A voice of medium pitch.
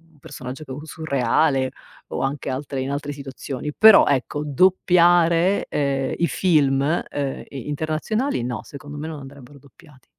Yes: medium, 145 Hz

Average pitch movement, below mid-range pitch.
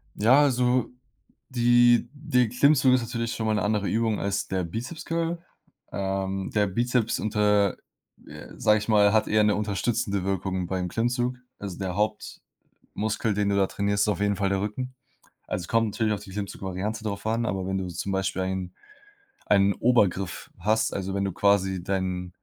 Yes: average, 3.2 semitones; low, 105 Hz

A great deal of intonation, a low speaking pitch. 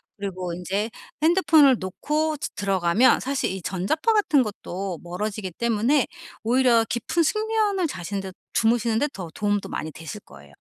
No: wide, 7.3 semitones; high, 215 Hz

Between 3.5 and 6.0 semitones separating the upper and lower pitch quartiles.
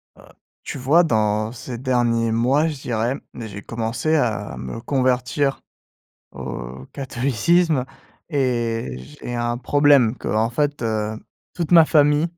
Yes: average, 4.4 semitones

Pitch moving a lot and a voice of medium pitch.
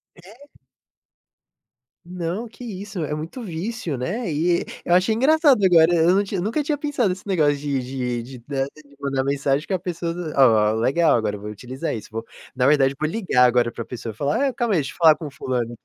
Yes: wide, 6.6 semitones; medium, 155 Hz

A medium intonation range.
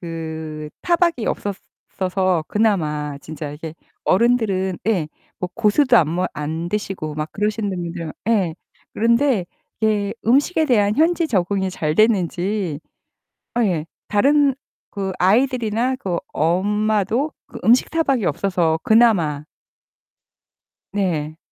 No: wide, 5.7 semitones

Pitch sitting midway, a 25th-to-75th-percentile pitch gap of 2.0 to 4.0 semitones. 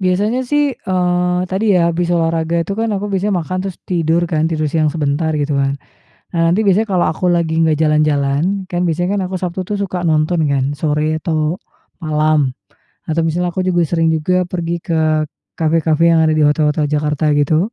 Yes: medium, 165 Hz; average, 2.8 semitones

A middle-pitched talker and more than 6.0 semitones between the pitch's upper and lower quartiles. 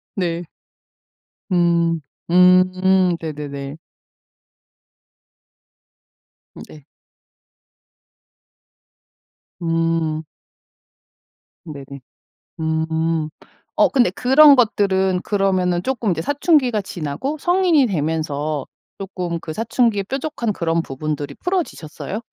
No: medium, 180 Hz; wide, 5.4 semitones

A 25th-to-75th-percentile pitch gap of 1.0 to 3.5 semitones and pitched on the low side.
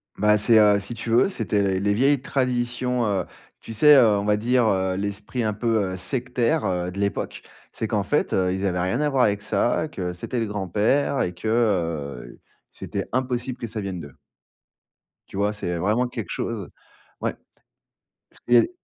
No: average, 3.9 semitones; low, 105 Hz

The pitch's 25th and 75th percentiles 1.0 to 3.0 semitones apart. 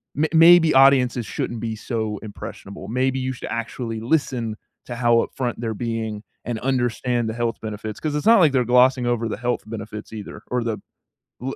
Yes: average, 2.7 semitones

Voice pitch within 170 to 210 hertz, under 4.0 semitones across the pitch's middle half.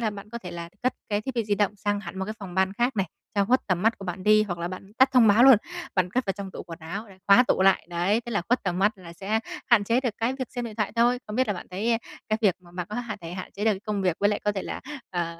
Yes: high, 205 Hz; average, 3.4 semitones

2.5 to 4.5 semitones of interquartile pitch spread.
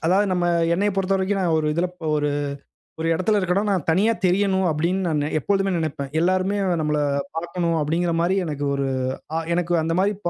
Yes: average, 3.0 semitones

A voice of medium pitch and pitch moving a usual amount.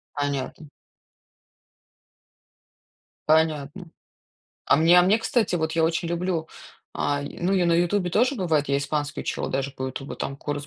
Yes: medium, 160 Hz; average, 3.6 semitones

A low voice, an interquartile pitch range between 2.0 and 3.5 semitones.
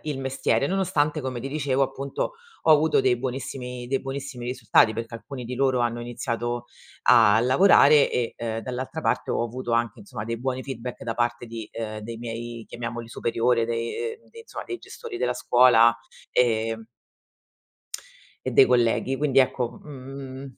Yes: low, 125 Hz; narrow, 2.6 semitones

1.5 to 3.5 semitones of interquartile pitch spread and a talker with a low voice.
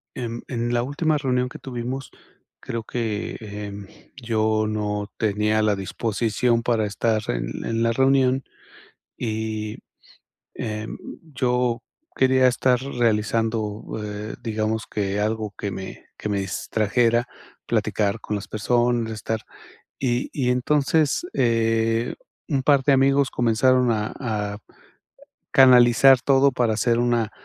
Yes: average, 2.7 semitones; low, 115 Hz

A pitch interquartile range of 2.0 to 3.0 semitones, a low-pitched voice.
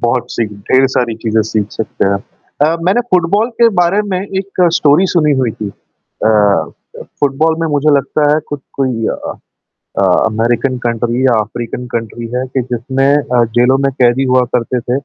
No: average, 4.4 semitones; low, 130 Hz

